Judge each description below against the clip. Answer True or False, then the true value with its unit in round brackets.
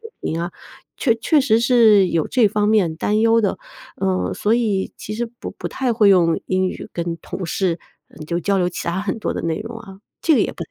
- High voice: True (205 Hz)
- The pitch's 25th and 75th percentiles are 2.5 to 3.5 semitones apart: False (4.3 semitones)